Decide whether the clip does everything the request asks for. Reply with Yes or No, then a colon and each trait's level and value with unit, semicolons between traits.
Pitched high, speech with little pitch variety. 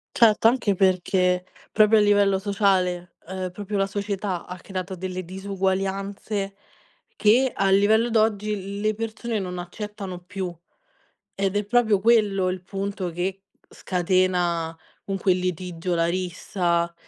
Yes: high, 195 Hz; narrow, 2.2 semitones